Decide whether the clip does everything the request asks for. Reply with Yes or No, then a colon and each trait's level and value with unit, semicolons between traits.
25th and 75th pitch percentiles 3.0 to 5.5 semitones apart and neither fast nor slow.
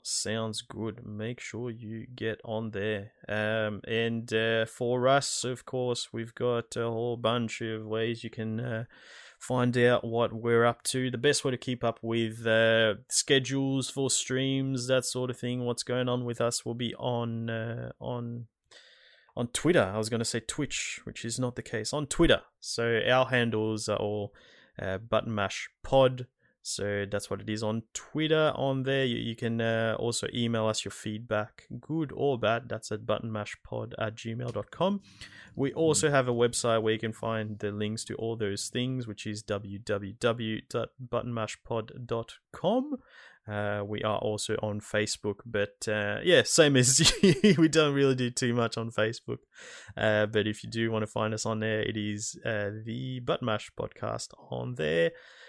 No: narrow, 2.5 semitones; average, 175 wpm